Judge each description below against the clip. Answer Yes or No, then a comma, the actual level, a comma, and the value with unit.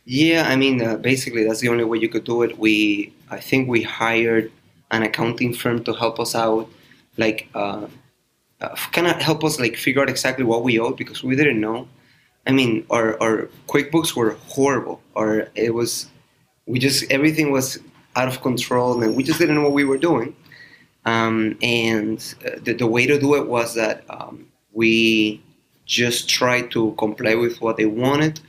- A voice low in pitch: Yes, low, 120 Hz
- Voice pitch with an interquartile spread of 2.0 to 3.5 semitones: Yes, average, 3.2 semitones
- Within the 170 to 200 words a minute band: Yes, average, 190 wpm